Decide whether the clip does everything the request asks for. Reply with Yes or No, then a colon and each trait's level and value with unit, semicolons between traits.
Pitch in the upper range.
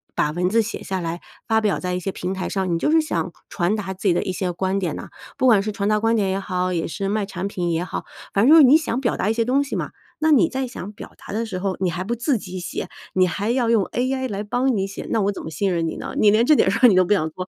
Yes: high, 200 Hz